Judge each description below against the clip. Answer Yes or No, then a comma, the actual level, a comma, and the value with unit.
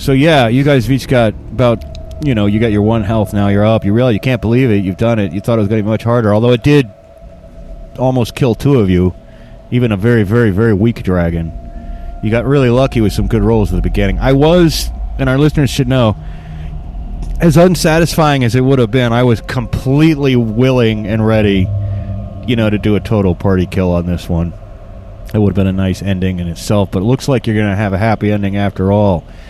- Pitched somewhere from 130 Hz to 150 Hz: No, low, 110 Hz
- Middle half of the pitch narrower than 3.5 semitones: No, average, 4.2 semitones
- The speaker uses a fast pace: Yes, fast, 235 wpm